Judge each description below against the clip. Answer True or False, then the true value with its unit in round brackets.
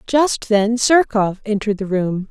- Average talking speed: True (155 wpm)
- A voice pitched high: True (215 Hz)